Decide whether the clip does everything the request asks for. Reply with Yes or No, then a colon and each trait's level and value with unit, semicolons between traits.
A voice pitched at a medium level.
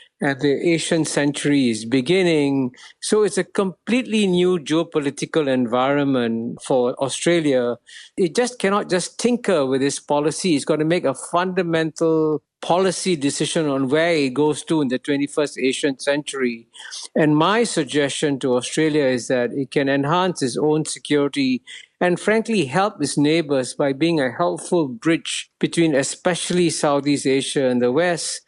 Yes: medium, 155 Hz